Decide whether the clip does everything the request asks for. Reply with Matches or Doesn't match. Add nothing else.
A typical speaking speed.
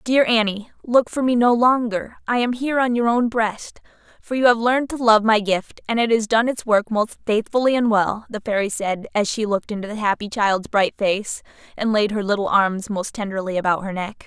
Doesn't match